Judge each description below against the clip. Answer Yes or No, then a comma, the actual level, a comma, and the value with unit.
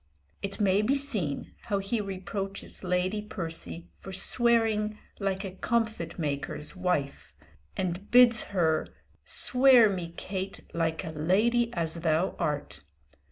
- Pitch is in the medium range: No, high, 195 Hz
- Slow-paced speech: Yes, slow, 125 wpm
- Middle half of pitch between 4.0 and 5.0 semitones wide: Yes, average, 4.3 semitones